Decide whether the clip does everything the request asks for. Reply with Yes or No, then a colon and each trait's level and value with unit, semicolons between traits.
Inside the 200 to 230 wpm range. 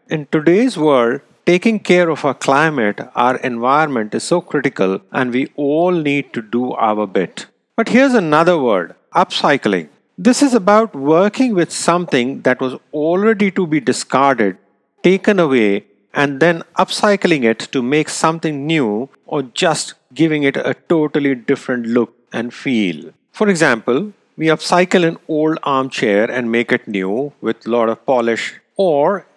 No: average, 155 wpm